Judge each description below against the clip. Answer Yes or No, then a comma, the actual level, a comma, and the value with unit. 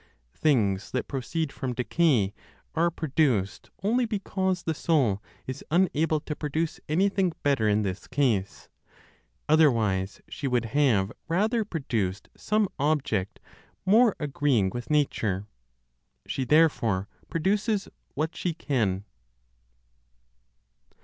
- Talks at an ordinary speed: No, slow, 110 wpm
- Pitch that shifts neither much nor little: No, wide, 7.1 semitones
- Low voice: No, medium, 145 Hz